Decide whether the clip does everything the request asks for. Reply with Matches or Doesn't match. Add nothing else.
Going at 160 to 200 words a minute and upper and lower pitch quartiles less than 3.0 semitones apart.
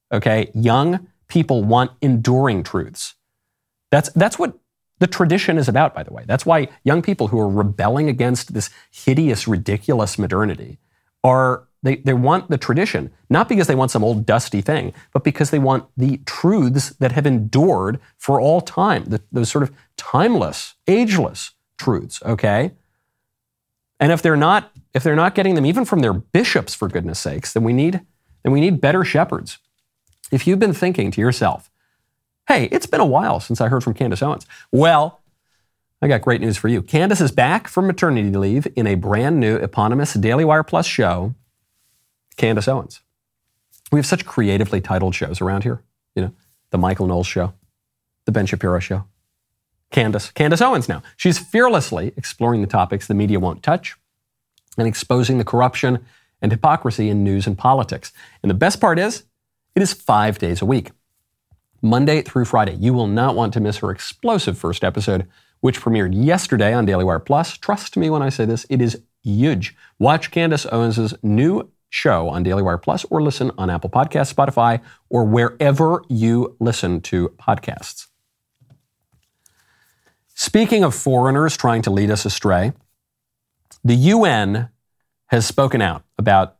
Doesn't match